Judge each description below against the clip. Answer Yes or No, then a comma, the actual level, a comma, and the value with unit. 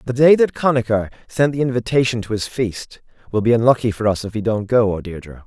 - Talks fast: Yes, fast, 230 wpm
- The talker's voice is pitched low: Yes, low, 115 Hz